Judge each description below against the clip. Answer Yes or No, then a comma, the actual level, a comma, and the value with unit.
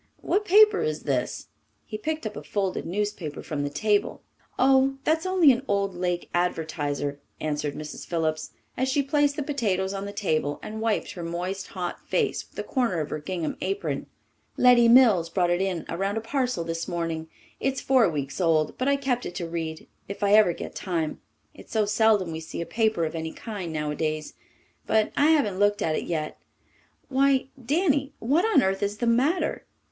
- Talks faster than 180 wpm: Yes, average, 190 wpm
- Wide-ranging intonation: Yes, wide, 7.6 semitones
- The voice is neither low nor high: No, high, 200 Hz